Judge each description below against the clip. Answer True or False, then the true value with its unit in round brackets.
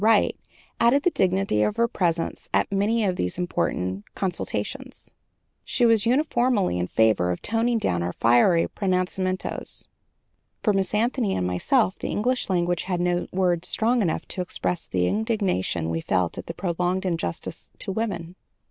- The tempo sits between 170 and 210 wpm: False (155 wpm)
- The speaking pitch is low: False (185 Hz)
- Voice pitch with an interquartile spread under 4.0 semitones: False (5.1 semitones)